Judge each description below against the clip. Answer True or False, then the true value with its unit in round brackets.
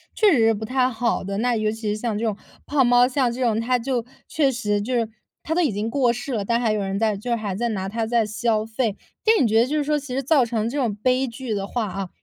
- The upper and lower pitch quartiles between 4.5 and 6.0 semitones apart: False (3.0 semitones)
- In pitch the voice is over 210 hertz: True (235 Hz)